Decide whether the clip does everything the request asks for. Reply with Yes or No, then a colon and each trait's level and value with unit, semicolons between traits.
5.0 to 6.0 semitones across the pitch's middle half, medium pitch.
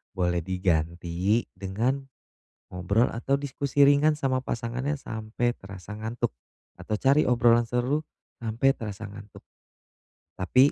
No: wide, 5.5 semitones; low, 115 Hz